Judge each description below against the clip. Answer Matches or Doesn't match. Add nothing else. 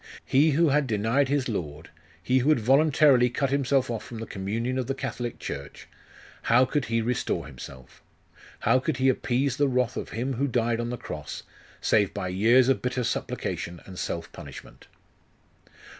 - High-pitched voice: Doesn't match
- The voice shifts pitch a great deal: Doesn't match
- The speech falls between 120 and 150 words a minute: Doesn't match